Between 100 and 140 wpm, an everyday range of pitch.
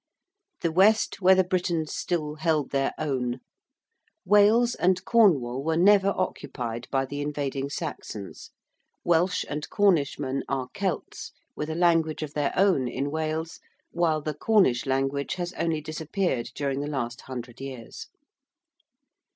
Yes: slow, 135 wpm; average, 4.6 semitones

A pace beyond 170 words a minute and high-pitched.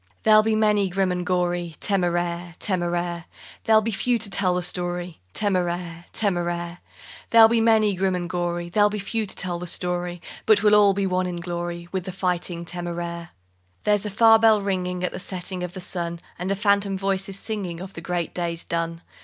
No: average, 195 wpm; medium, 180 Hz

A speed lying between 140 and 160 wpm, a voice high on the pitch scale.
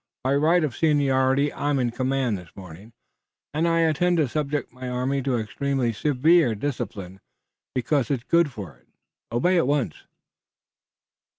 No: average, 150 wpm; low, 135 Hz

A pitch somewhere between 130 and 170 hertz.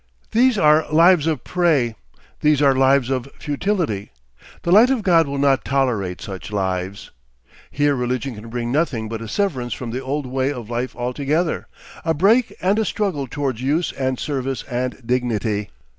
Yes: low, 135 Hz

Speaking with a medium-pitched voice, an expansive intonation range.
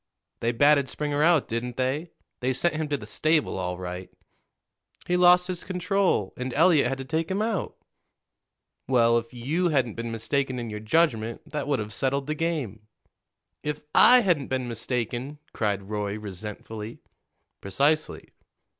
No: low, 130 Hz; wide, 5.7 semitones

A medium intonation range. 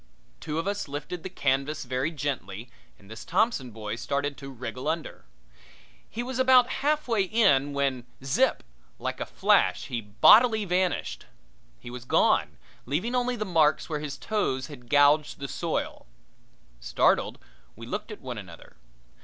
No: wide, 8.0 semitones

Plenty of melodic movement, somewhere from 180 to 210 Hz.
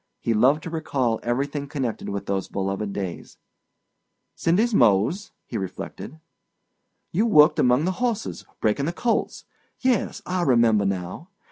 No: wide, 8.2 semitones; low, 135 Hz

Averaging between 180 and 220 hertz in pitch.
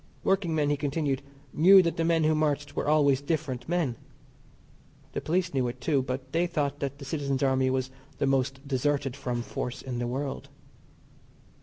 No: medium, 140 Hz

